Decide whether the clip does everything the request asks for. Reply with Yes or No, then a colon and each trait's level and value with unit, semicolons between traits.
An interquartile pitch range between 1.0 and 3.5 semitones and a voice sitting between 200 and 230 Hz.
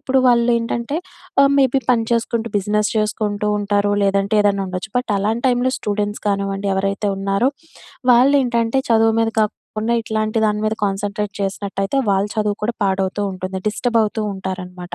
Yes: average, 2.8 semitones; high, 210 Hz